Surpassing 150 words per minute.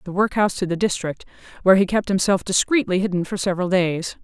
Yes: average, 200 wpm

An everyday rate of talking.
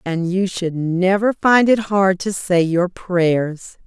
Yes: average, 170 wpm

